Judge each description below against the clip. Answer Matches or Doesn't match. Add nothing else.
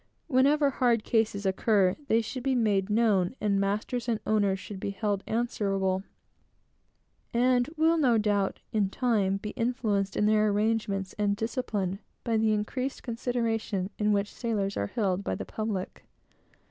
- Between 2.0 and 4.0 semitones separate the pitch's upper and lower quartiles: Matches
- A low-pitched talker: Doesn't match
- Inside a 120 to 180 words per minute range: Matches